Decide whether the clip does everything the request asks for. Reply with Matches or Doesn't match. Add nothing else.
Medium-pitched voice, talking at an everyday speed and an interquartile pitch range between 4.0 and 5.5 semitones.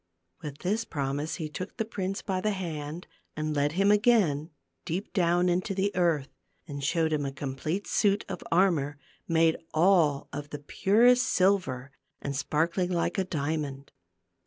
Matches